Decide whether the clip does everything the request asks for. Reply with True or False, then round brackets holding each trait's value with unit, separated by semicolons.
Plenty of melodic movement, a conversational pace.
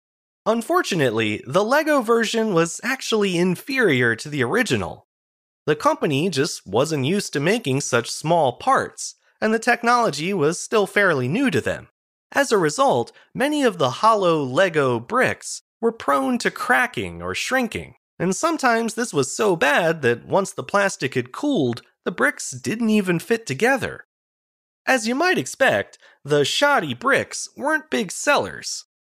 True (8.7 semitones; 150 wpm)